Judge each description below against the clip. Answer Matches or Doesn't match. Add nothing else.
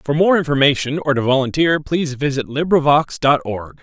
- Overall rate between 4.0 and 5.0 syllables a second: Doesn't match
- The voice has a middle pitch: Matches